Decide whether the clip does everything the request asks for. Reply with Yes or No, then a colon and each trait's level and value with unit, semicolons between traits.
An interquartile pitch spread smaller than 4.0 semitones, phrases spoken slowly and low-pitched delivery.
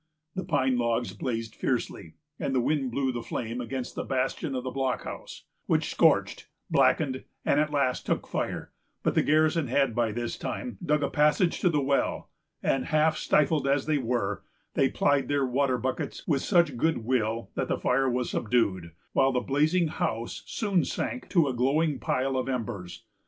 No: average, 3.6 semitones; average, 180 wpm; low, 130 Hz